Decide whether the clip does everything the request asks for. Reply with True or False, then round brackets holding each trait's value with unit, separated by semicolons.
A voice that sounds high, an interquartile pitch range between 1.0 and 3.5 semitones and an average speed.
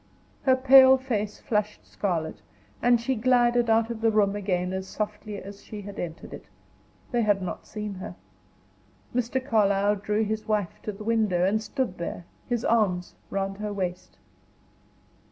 True (210 Hz; 2.9 semitones; 160 wpm)